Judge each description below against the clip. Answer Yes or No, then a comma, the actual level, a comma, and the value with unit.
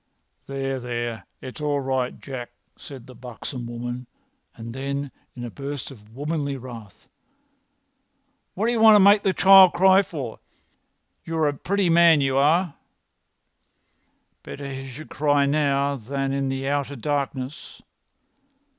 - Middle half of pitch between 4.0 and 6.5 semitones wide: No, average, 3.1 semitones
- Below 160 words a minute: Yes, slow, 135 wpm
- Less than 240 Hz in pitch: Yes, medium, 140 Hz